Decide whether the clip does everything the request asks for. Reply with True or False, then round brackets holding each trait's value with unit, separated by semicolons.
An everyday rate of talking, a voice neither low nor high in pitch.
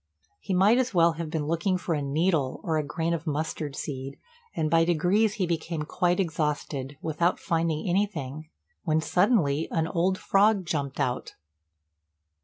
True (160 wpm; 165 Hz)